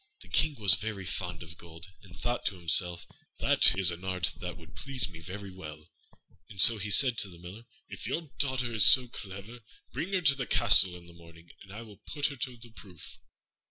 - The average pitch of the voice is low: Yes, very low, 95 Hz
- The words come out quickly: Yes, fast, 225 wpm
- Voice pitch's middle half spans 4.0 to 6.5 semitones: Yes, average, 5.3 semitones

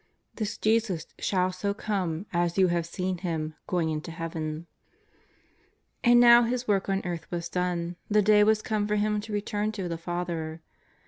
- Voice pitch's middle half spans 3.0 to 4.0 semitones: Yes, average, 3.7 semitones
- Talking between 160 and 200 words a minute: Yes, average, 175 wpm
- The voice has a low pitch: No, medium, 185 Hz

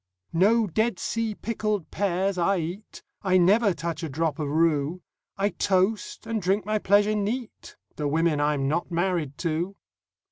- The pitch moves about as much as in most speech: Yes, average, 4.2 semitones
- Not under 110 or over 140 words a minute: No, average, 155 wpm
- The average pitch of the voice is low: No, medium, 185 Hz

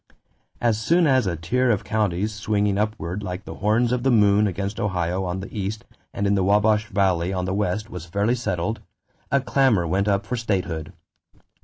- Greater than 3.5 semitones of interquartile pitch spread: No, average, 2.9 semitones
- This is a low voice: Yes, low, 100 Hz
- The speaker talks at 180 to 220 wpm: Yes, average, 190 wpm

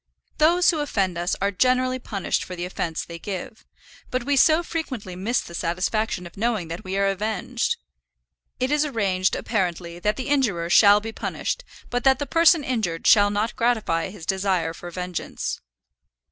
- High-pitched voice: Yes, high, 205 Hz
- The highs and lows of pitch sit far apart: Yes, wide, 5.9 semitones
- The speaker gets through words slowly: No, average, 175 wpm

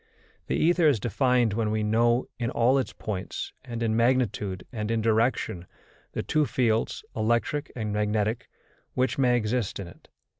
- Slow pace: No, average, 160 wpm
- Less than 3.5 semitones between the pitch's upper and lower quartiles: Yes, average, 2.8 semitones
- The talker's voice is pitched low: Yes, low, 115 Hz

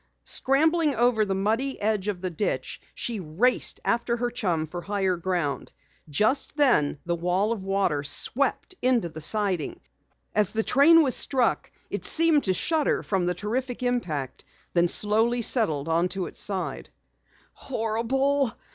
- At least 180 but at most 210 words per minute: No, average, 145 wpm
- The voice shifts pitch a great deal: Yes, wide, 5.8 semitones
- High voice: Yes, high, 210 Hz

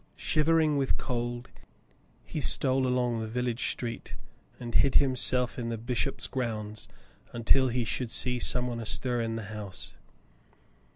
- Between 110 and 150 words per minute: Yes, average, 140 wpm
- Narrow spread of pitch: Yes, narrow, 1.9 semitones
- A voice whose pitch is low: Yes, low, 120 Hz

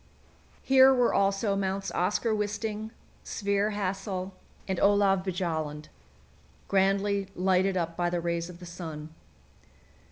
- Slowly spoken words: Yes, slow, 120 wpm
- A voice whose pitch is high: Yes, high, 195 Hz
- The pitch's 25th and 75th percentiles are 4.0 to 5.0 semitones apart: No, narrow, 2.5 semitones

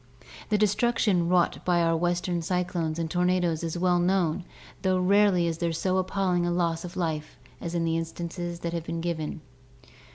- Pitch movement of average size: No, narrow, 1.6 semitones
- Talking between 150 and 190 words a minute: Yes, average, 185 wpm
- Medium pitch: Yes, medium, 175 Hz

